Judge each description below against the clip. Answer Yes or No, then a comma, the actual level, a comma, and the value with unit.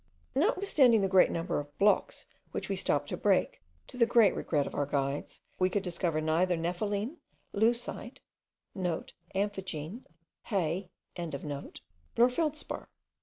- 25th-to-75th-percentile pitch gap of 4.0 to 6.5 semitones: Yes, average, 5.2 semitones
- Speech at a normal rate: No, slow, 130 wpm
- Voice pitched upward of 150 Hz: Yes, high, 190 Hz